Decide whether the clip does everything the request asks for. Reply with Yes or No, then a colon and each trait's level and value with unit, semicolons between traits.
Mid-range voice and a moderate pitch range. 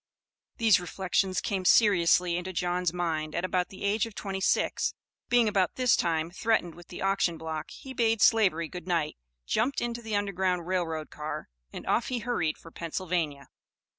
Yes: medium, 180 Hz; average, 3.7 semitones